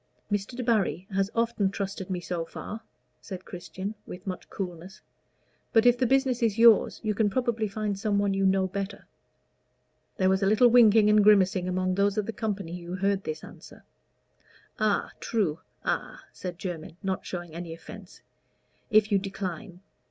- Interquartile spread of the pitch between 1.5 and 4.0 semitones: Yes, average, 2.7 semitones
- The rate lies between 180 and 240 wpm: No, average, 165 wpm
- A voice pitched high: Yes, high, 195 Hz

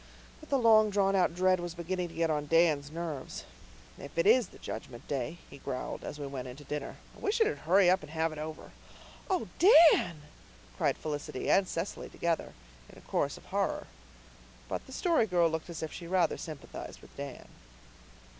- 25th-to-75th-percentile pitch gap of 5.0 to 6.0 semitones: No, average, 4.3 semitones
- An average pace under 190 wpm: No, average, 195 wpm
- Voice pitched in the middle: Yes, medium, 170 Hz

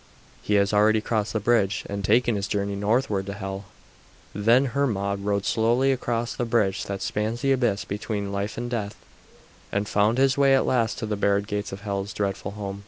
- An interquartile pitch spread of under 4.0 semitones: Yes, average, 2.7 semitones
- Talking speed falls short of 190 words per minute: No, average, 195 wpm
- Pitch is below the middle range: Yes, low, 105 Hz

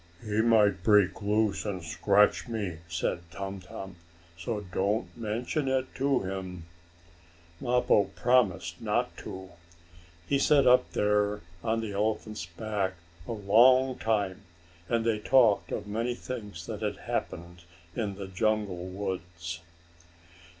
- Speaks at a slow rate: Yes, slow, 130 wpm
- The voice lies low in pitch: Yes, low, 105 Hz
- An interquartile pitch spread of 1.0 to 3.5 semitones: Yes, average, 3.2 semitones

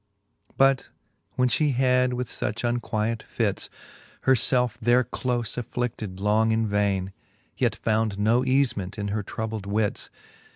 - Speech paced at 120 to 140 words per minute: Yes, slow, 135 wpm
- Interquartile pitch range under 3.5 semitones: Yes, average, 3.1 semitones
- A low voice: Yes, low, 115 Hz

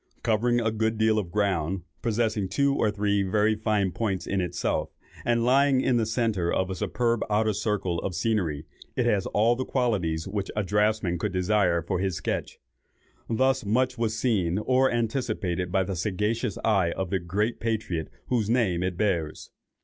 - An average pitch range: Yes, average, 3.5 semitones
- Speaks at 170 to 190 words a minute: Yes, average, 175 wpm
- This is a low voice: Yes, low, 105 Hz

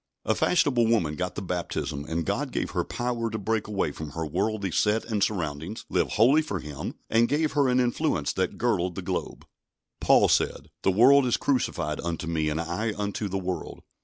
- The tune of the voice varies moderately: No, wide, 5.8 semitones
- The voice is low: Yes, low, 100 Hz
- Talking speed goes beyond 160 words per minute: Yes, average, 195 wpm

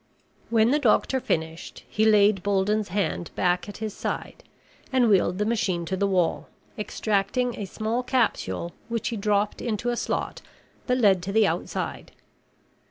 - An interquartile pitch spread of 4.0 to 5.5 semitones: No, average, 3.2 semitones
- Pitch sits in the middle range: No, high, 210 Hz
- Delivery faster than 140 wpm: Yes, average, 160 wpm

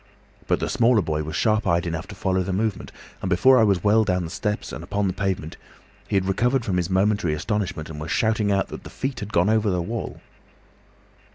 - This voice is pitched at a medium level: No, very low, 95 Hz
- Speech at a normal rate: No, fast, 225 wpm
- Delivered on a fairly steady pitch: No, average, 3.5 semitones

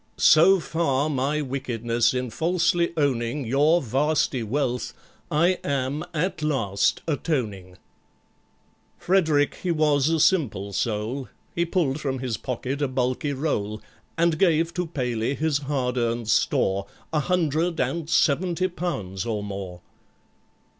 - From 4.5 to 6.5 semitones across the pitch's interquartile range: Yes, average, 5.1 semitones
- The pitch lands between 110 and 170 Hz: Yes, medium, 140 Hz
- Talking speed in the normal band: No, slow, 125 wpm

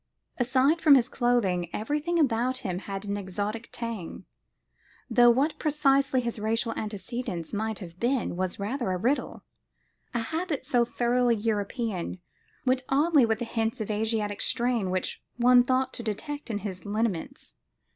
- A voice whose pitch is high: Yes, high, 235 Hz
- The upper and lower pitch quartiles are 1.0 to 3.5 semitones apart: No, average, 4.0 semitones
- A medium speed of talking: Yes, average, 150 wpm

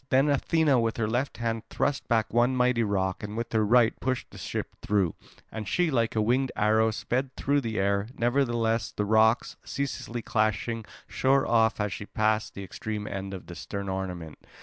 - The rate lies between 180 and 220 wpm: Yes, average, 190 wpm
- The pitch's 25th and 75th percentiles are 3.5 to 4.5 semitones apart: No, average, 3.0 semitones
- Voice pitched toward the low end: Yes, low, 115 Hz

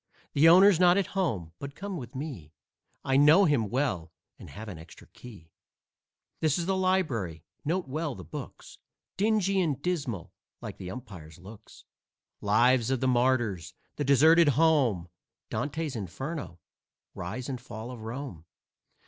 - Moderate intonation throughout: No, wide, 7.5 semitones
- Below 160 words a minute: Yes, average, 150 wpm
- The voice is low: Yes, low, 130 Hz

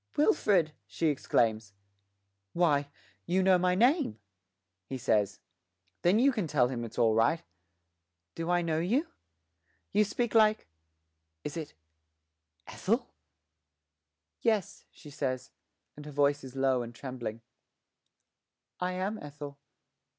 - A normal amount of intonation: No, wide, 6.4 semitones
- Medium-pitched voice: Yes, medium, 150 Hz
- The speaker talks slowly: Yes, slow, 120 wpm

